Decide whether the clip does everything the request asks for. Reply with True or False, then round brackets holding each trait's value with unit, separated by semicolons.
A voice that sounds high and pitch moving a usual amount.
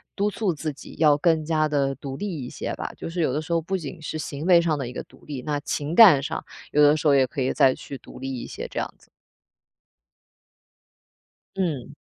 False (150 Hz; 3.1 semitones)